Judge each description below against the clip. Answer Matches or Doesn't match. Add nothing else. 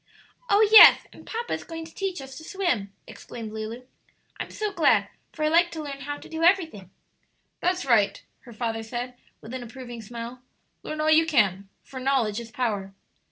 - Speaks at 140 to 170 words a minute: Doesn't match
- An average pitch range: Doesn't match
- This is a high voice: Matches